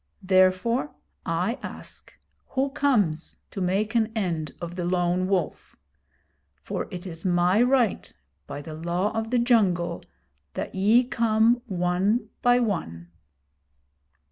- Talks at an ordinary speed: No, slow, 125 wpm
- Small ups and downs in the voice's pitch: No, average, 4.7 semitones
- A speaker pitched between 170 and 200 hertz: Yes, high, 190 Hz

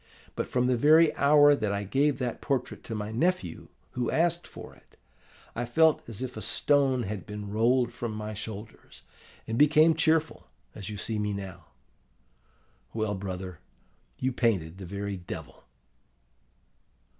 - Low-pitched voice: Yes, low, 115 Hz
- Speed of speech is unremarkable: Yes, average, 155 wpm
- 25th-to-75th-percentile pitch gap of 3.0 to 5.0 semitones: No, wide, 5.6 semitones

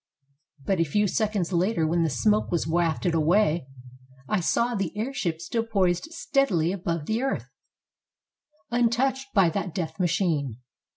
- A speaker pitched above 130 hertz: Yes, medium, 185 Hz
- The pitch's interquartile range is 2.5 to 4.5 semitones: No, average, 4.9 semitones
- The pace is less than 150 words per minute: Yes, average, 140 wpm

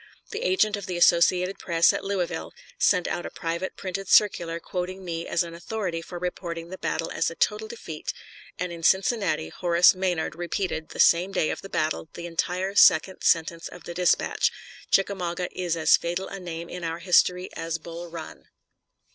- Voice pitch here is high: No, medium, 175 Hz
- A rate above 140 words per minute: Yes, average, 180 wpm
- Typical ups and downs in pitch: No, narrow, 2.0 semitones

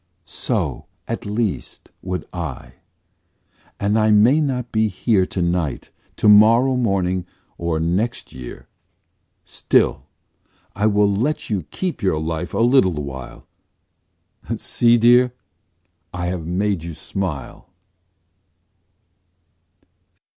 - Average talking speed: No, slow, 110 wpm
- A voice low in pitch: Yes, low, 100 Hz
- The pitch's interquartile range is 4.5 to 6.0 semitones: Yes, average, 5.0 semitones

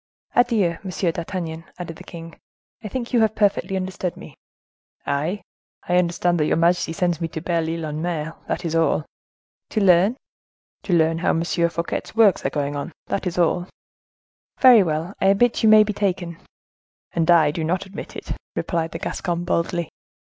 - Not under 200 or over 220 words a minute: No, average, 180 wpm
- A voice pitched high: No, medium, 175 Hz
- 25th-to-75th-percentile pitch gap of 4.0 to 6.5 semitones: No, average, 2.8 semitones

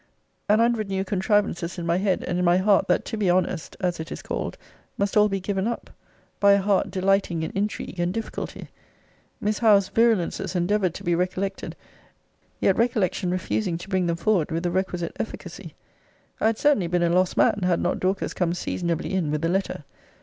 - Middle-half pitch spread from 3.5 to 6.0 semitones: No, average, 2.7 semitones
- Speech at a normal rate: Yes, average, 195 wpm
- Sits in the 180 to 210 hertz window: Yes, medium, 185 Hz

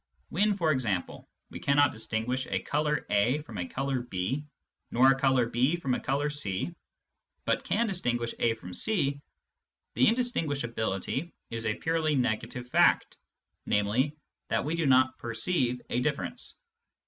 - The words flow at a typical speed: Yes, average, 150 wpm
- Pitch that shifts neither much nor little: Yes, average, 4.4 semitones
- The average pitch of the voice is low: Yes, low, 130 Hz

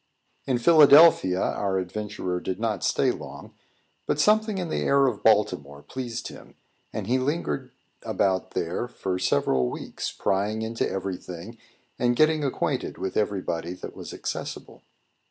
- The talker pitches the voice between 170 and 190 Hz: No, low, 105 Hz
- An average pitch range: No, wide, 6.2 semitones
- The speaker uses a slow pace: No, average, 145 wpm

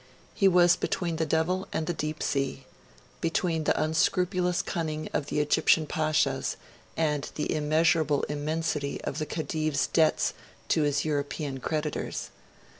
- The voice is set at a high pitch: No, medium, 155 Hz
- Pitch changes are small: Yes, narrow, 1.8 semitones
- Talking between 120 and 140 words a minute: Yes, slow, 135 wpm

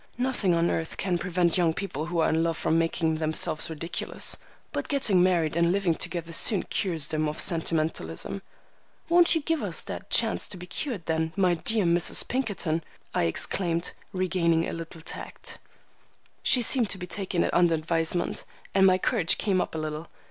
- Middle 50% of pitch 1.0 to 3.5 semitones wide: Yes, average, 2.9 semitones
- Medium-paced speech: Yes, average, 180 wpm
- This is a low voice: No, medium, 170 Hz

